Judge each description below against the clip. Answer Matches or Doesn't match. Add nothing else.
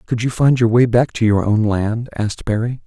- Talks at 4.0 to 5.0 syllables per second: Doesn't match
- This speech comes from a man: Matches